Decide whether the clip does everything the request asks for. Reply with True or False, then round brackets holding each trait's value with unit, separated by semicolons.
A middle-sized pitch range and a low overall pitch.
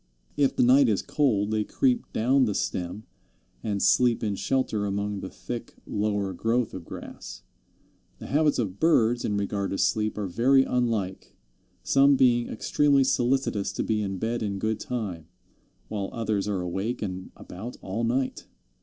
True (3.8 semitones; 110 Hz)